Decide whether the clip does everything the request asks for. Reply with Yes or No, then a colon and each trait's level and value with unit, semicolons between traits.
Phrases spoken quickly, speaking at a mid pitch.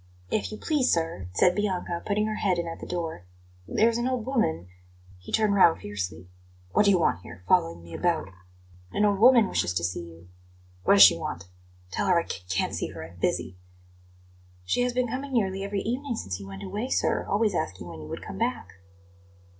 Yes: fast, 210 wpm; medium, 170 Hz